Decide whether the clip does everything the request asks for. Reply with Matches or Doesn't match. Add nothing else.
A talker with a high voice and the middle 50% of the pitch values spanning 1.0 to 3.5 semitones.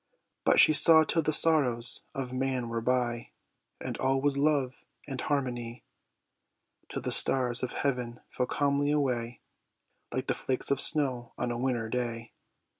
Doesn't match